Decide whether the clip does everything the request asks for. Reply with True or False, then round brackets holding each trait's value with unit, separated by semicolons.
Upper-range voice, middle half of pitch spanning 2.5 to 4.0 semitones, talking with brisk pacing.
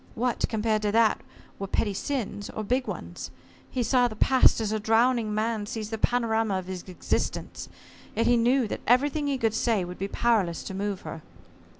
False (225 Hz; 2.9 semitones; 195 wpm)